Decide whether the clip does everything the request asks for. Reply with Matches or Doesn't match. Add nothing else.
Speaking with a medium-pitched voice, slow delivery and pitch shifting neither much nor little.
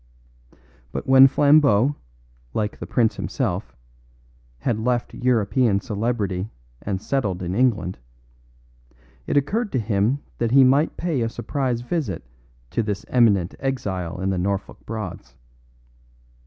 Doesn't match